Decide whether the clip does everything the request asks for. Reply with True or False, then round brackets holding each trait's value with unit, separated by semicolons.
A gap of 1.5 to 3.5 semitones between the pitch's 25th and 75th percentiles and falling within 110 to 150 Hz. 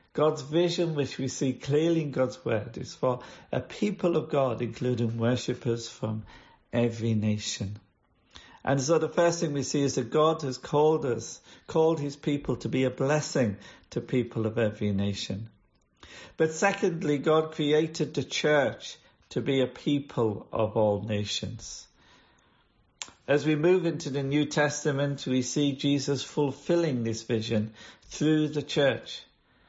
False (5.0 semitones; 135 Hz)